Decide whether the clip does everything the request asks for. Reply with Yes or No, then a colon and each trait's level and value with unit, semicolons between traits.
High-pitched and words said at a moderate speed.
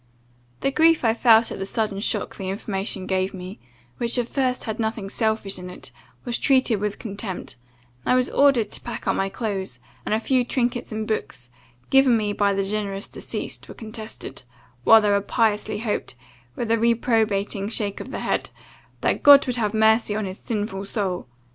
Yes: high, 215 Hz; average, 185 wpm